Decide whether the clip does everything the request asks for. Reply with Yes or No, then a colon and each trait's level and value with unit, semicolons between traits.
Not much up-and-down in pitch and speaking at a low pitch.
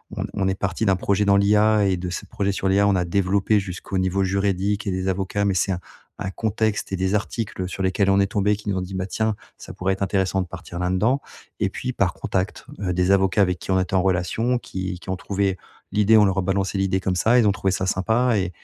Yes: narrow, 1.5 semitones; very low, 95 Hz